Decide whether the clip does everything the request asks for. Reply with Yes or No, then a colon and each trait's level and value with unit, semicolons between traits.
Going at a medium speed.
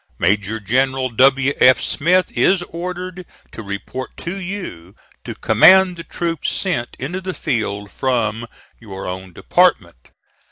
No: slow, 130 wpm